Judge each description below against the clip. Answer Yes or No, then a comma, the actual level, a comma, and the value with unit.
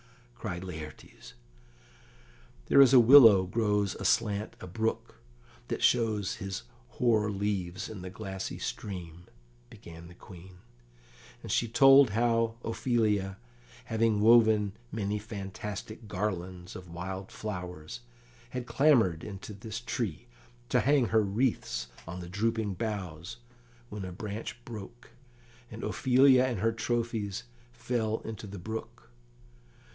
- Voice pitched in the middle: No, low, 105 Hz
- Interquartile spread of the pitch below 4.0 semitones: Yes, average, 3.5 semitones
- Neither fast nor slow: No, slow, 120 wpm